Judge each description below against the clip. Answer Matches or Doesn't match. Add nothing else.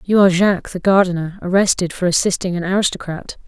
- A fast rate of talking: Doesn't match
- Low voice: Doesn't match